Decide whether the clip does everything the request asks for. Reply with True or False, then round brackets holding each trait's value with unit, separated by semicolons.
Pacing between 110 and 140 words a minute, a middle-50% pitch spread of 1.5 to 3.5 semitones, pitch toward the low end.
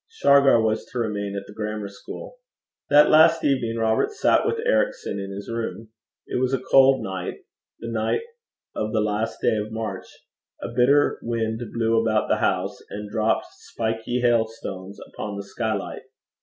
False (165 wpm; 3.1 semitones; 115 Hz)